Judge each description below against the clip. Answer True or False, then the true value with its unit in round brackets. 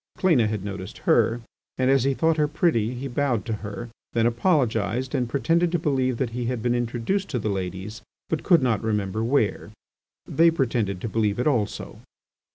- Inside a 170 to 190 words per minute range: True (185 wpm)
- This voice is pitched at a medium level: False (120 Hz)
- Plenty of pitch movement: False (4.3 semitones)